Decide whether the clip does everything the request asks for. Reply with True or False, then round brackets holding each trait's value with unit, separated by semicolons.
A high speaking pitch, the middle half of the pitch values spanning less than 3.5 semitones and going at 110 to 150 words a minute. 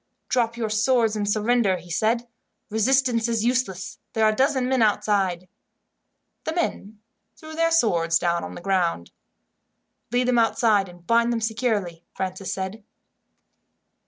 False (220 Hz; 4.2 semitones; 145 wpm)